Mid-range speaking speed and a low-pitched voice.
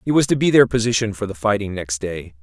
No: fast, 270 wpm; low, 105 Hz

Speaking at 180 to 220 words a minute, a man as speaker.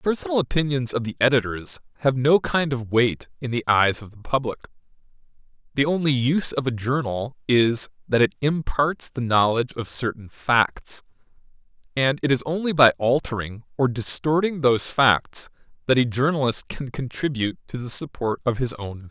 No: average, 170 wpm; male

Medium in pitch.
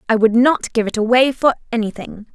No: high, 235 Hz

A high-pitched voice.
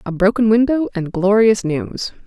Yes: high, 210 Hz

